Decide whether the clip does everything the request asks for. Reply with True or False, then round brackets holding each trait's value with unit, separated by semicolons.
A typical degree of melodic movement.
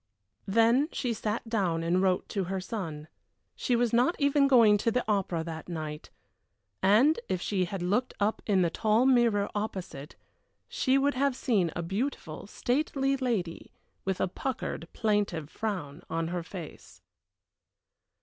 False (5.7 semitones)